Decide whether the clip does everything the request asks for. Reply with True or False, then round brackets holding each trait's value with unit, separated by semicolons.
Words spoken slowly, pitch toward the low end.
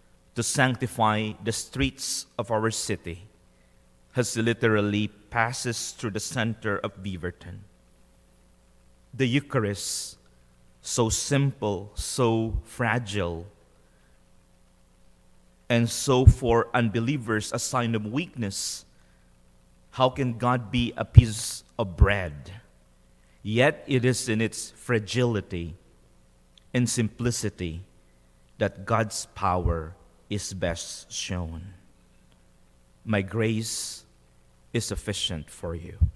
True (95 wpm; 100 Hz)